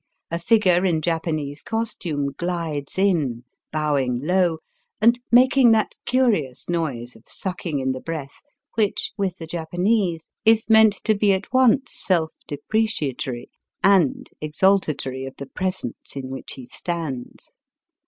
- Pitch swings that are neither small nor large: No, wide, 6.0 semitones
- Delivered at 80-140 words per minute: Yes, slow, 135 wpm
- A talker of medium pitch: Yes, medium, 170 Hz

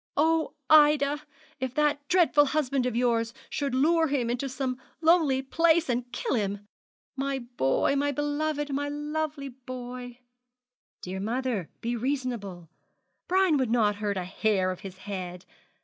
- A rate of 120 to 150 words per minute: Yes, average, 145 wpm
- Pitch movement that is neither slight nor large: Yes, average, 4.1 semitones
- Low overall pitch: No, very high, 260 Hz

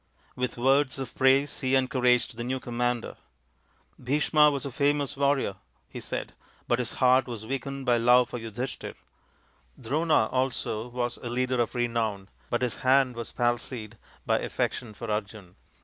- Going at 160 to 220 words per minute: Yes, average, 165 wpm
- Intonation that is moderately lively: No, narrow, 2.1 semitones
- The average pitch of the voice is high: No, low, 125 Hz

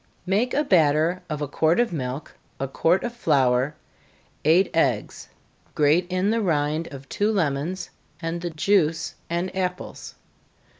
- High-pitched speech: No, medium, 165 Hz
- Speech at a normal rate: Yes, average, 145 wpm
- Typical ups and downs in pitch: Yes, average, 4.1 semitones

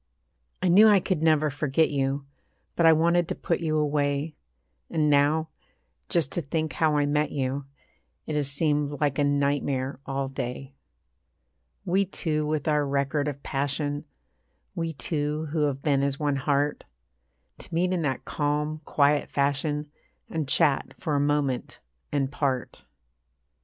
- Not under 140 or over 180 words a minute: Yes, average, 150 wpm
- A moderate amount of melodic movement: No, narrow, 1.9 semitones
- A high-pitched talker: No, medium, 145 Hz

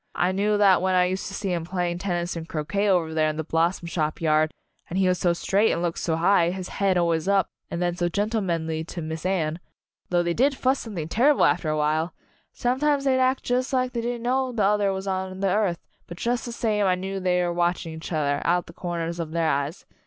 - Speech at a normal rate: No, fast, 240 wpm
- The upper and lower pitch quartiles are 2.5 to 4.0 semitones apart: Yes, average, 3.5 semitones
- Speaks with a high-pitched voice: No, medium, 180 Hz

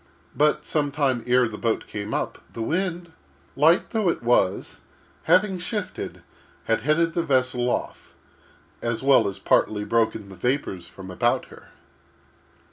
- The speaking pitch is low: Yes, low, 130 Hz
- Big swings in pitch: Yes, wide, 6.7 semitones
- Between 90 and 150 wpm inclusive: Yes, average, 145 wpm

